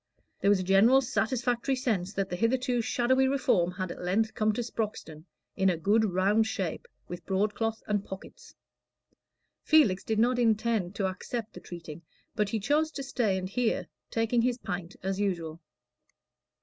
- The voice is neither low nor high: No, high, 215 Hz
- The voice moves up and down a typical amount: Yes, average, 4.2 semitones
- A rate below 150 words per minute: No, average, 165 wpm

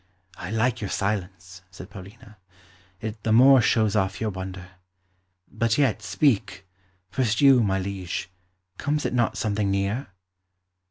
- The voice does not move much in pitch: No, average, 3.6 semitones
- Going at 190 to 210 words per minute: No, average, 140 wpm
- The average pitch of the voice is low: Yes, low, 105 Hz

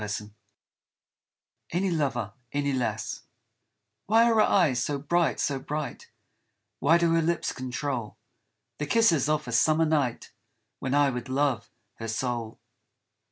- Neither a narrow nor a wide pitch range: Yes, average, 4.8 semitones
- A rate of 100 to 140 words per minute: Yes, slow, 135 wpm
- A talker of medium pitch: Yes, medium, 145 Hz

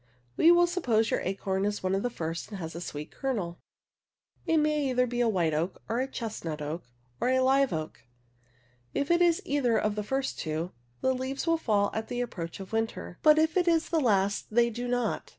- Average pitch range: No, wide, 6.1 semitones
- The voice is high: Yes, high, 230 Hz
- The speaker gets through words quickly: Yes, fast, 215 wpm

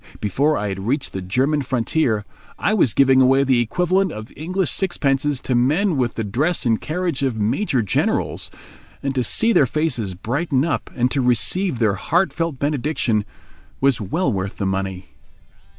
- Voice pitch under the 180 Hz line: Yes, low, 135 Hz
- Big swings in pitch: Yes, wide, 5.9 semitones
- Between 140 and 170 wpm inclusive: Yes, average, 165 wpm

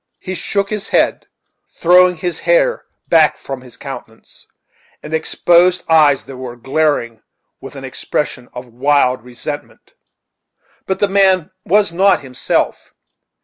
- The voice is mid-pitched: Yes, medium, 160 Hz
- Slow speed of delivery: Yes, slow, 130 wpm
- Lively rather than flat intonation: Yes, wide, 6.3 semitones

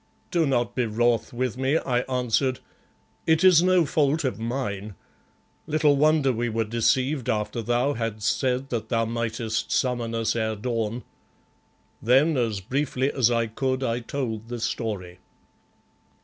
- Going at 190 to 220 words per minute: No, average, 150 wpm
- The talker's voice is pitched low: Yes, low, 120 Hz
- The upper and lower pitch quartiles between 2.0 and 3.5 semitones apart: Yes, average, 3.1 semitones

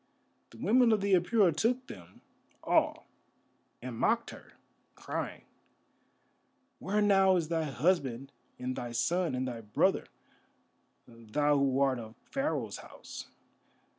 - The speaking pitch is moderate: Yes, medium, 150 Hz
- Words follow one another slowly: Yes, slow, 125 wpm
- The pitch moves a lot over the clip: Yes, wide, 7.9 semitones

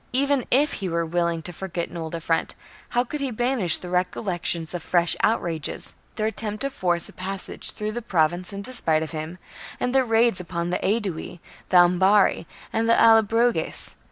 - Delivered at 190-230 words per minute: Yes, average, 195 wpm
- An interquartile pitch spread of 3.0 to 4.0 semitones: No, average, 5.0 semitones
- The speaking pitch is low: No, high, 190 Hz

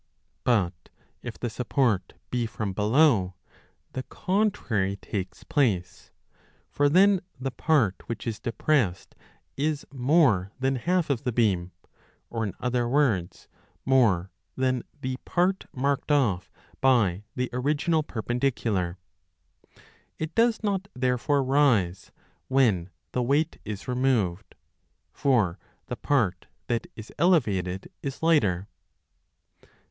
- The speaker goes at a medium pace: No, slow, 115 wpm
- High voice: No, low, 125 Hz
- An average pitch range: No, wide, 6.1 semitones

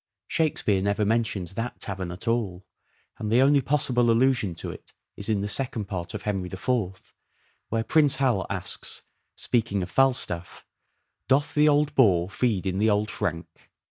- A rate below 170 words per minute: No, average, 175 wpm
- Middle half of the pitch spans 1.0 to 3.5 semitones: No, average, 4.8 semitones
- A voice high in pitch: No, low, 110 Hz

